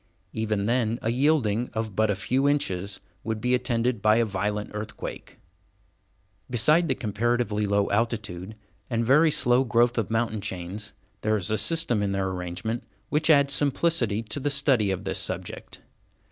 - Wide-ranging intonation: No, average, 3.5 semitones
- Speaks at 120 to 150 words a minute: No, average, 160 wpm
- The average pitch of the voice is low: Yes, low, 110 Hz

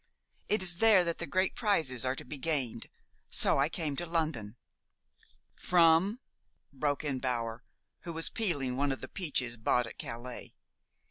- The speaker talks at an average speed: Yes, average, 170 wpm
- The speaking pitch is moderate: Yes, medium, 150 Hz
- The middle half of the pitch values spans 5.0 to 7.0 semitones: Yes, average, 5.3 semitones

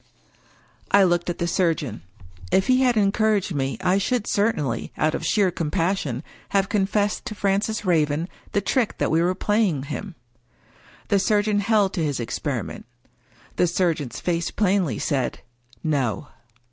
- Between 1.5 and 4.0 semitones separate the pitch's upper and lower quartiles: No, average, 4.7 semitones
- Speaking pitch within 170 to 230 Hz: Yes, medium, 185 Hz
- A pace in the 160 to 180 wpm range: No, average, 145 wpm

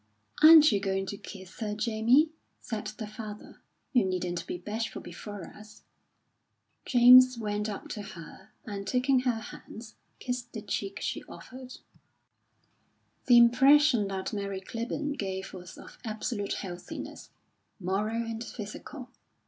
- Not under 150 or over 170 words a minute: No, slow, 135 wpm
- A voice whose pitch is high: Yes, high, 215 Hz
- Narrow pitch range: No, average, 3.8 semitones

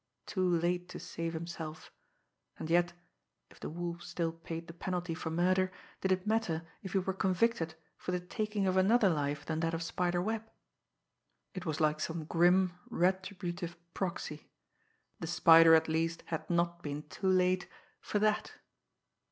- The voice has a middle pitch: Yes, medium, 175 Hz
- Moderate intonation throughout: No, narrow, 2.2 semitones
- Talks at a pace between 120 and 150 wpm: No, average, 160 wpm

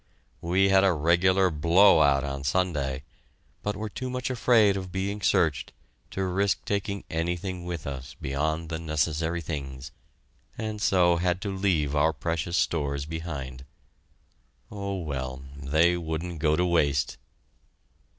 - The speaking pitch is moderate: No, very low, 85 Hz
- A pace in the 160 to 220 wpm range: No, average, 140 wpm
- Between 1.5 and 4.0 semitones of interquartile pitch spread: No, average, 4.4 semitones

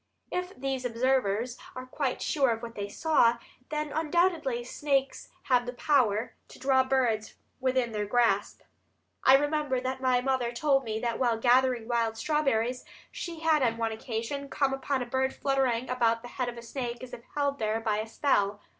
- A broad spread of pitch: No, average, 2.8 semitones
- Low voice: No, very high, 255 Hz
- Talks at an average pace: Yes, average, 180 wpm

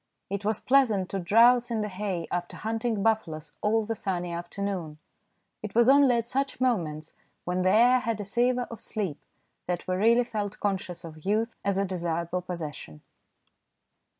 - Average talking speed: Yes, average, 170 wpm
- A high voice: Yes, high, 200 Hz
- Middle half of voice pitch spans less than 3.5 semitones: No, average, 4.5 semitones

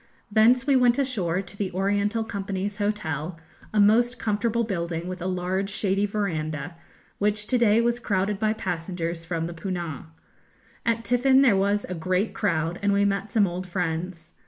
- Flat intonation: No, average, 3.5 semitones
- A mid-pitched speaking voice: No, high, 200 Hz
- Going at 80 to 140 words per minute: No, average, 170 wpm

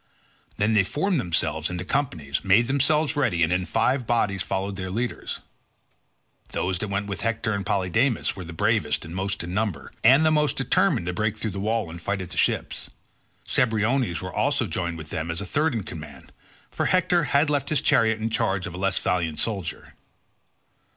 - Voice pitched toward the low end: Yes, low, 100 Hz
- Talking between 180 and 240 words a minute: Yes, average, 190 wpm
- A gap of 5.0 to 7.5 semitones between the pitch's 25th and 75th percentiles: Yes, wide, 5.6 semitones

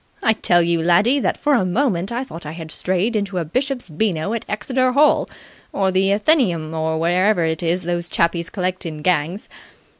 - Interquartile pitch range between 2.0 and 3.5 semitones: No, average, 4.7 semitones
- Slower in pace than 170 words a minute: No, average, 190 wpm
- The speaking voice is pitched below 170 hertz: No, medium, 185 Hz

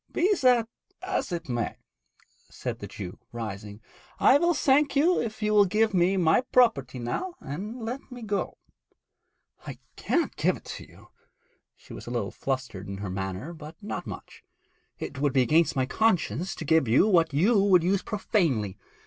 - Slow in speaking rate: No, average, 175 wpm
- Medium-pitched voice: Yes, medium, 170 Hz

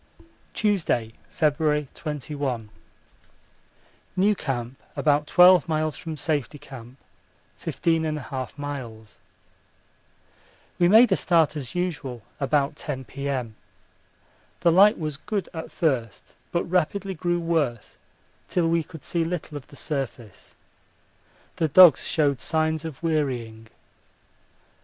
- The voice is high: No, medium, 150 Hz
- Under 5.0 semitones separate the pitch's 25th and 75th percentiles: Yes, average, 4.1 semitones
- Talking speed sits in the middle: No, slow, 115 wpm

